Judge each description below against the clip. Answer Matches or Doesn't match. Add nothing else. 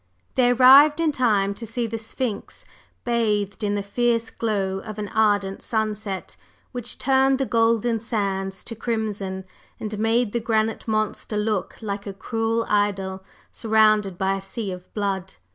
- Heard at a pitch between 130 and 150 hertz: Doesn't match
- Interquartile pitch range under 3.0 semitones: Matches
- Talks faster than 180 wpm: Doesn't match